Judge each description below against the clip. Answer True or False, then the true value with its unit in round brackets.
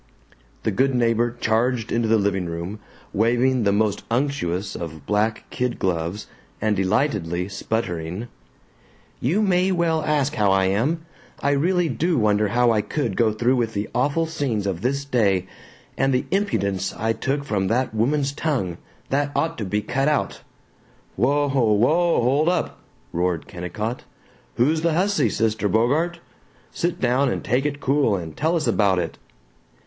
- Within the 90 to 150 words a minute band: False (160 wpm)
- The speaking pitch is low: True (120 Hz)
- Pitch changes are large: True (5.8 semitones)